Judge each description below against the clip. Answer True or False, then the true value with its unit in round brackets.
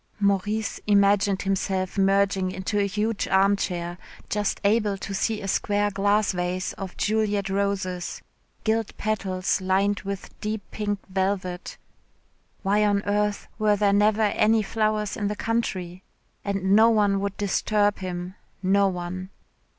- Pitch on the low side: False (200 Hz)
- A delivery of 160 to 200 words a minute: False (135 wpm)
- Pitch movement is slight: True (1.6 semitones)